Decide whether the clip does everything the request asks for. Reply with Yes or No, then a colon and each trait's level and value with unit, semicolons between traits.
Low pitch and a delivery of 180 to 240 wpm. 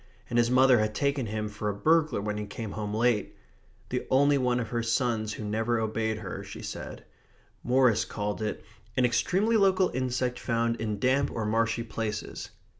Yes: low, 115 Hz; average, 185 wpm